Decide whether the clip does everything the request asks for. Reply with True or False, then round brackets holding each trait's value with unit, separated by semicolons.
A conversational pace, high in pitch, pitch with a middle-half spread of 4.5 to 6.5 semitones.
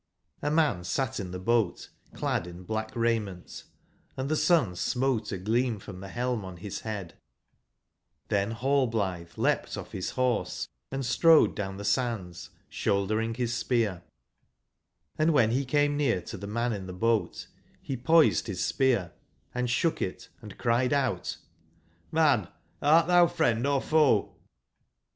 False (150 wpm; 115 Hz; 5.0 semitones)